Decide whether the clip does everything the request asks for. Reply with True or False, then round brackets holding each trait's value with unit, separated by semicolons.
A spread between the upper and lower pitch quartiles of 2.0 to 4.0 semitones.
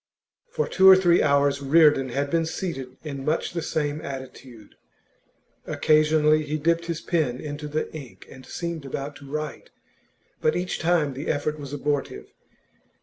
True (2.6 semitones)